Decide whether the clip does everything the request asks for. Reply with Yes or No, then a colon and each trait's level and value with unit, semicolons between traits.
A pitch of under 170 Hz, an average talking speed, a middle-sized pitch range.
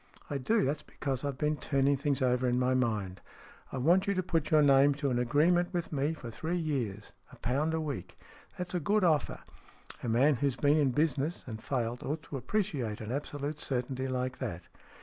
No: medium, 140 Hz; fast, 210 wpm; average, 3.6 semitones